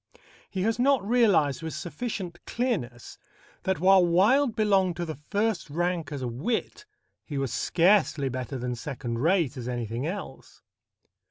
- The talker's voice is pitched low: No, medium, 175 Hz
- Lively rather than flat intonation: Yes, wide, 7.2 semitones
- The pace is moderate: Yes, average, 150 wpm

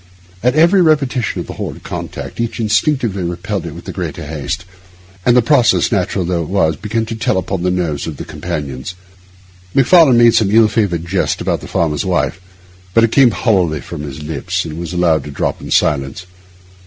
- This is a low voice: Yes, very low, 95 Hz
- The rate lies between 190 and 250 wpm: Yes, average, 195 wpm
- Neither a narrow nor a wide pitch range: No, wide, 6.1 semitones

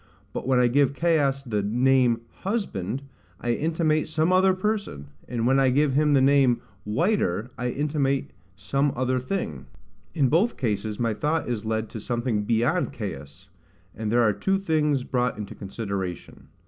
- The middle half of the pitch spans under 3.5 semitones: No, wide, 5.4 semitones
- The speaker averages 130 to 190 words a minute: Yes, average, 160 wpm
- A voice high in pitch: No, low, 130 Hz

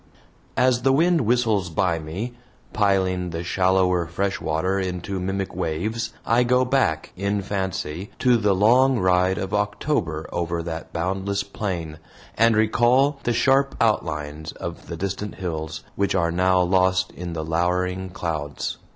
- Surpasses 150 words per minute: No, average, 145 wpm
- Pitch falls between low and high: No, very low, 95 Hz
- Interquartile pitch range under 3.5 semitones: No, average, 4.0 semitones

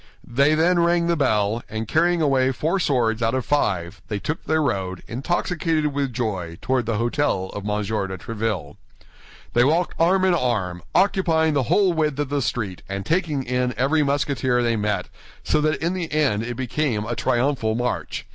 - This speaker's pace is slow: No, average, 185 wpm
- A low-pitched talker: Yes, low, 130 Hz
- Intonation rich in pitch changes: Yes, wide, 6.0 semitones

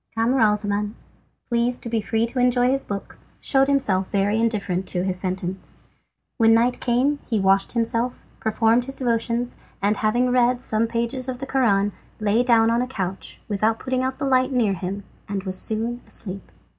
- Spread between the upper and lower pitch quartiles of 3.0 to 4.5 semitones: Yes, average, 3.5 semitones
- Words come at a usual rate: Yes, average, 175 wpm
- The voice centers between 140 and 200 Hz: No, high, 230 Hz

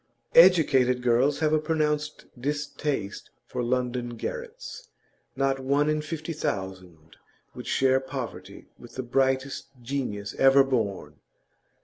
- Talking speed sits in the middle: No, slow, 115 wpm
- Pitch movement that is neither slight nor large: Yes, average, 3.8 semitones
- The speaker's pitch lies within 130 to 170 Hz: Yes, low, 135 Hz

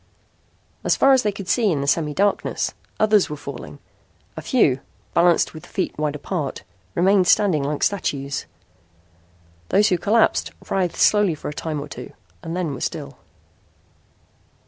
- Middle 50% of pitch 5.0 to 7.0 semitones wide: Yes, wide, 5.5 semitones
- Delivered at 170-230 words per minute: No, average, 145 wpm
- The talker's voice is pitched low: No, medium, 170 Hz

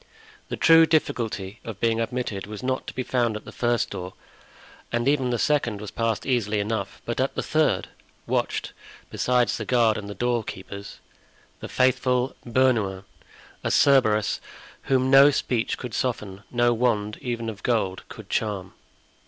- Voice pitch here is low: Yes, low, 115 Hz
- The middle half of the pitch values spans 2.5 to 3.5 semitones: Yes, average, 3.1 semitones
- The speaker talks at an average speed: Yes, average, 160 wpm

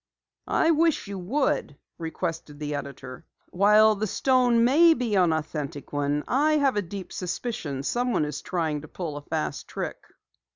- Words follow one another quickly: No, average, 160 wpm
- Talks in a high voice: No, medium, 180 Hz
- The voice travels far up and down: Yes, wide, 8.7 semitones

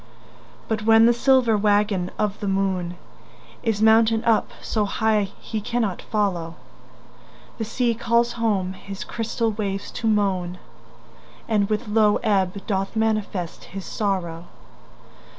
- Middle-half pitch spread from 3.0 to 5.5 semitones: No, narrow, 2.4 semitones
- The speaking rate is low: Yes, slow, 130 wpm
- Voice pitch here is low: No, high, 210 Hz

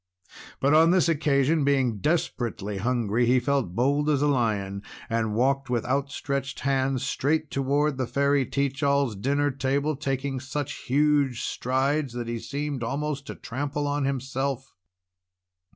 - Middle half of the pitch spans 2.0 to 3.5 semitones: Yes, narrow, 2.4 semitones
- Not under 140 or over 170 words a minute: Yes, average, 145 wpm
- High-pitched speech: No, low, 135 Hz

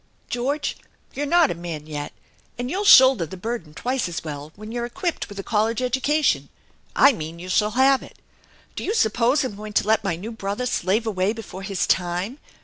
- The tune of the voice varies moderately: No, wide, 5.8 semitones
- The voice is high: Yes, high, 220 Hz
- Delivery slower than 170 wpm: No, fast, 205 wpm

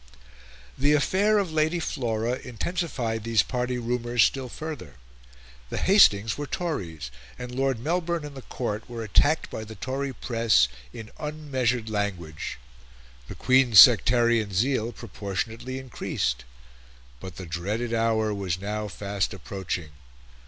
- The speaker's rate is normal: No, slow, 130 wpm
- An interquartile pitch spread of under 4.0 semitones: No, average, 4.6 semitones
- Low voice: Yes, low, 115 Hz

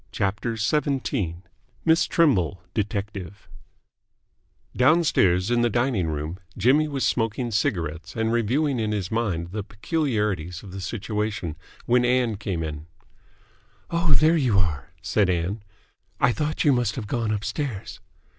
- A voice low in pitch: Yes, low, 105 Hz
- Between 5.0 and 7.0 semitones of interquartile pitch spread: Yes, average, 5.3 semitones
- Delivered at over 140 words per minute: No, slow, 135 wpm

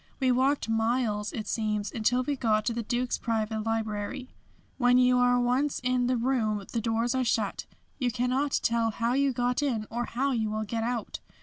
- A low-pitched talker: No, high, 240 Hz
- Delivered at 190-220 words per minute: Yes, average, 195 wpm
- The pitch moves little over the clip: Yes, narrow, 2.2 semitones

